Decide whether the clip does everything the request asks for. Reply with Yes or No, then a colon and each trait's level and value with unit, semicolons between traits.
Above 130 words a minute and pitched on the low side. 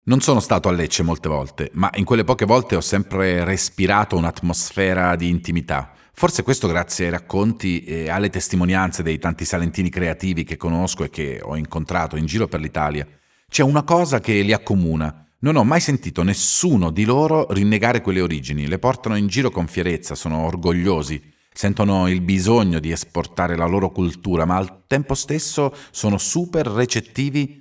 Yes: fast, 170 wpm; very low, 95 Hz